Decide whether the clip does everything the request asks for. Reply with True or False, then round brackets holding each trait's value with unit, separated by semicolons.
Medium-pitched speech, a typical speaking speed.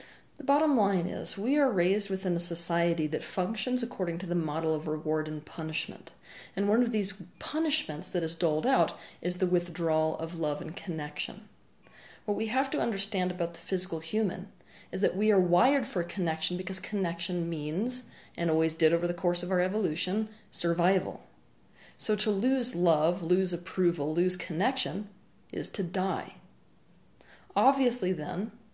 True (180 Hz; 165 wpm)